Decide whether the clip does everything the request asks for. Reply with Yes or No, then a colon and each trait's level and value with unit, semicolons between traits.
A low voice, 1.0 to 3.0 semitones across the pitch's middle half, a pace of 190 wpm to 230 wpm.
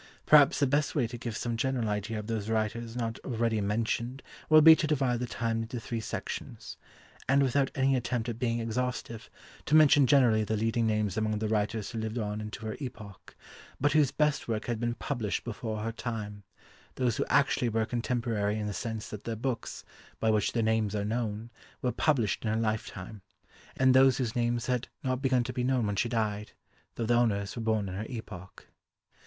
Yes: low, 115 Hz; narrow, 2.6 semitones; fast, 205 wpm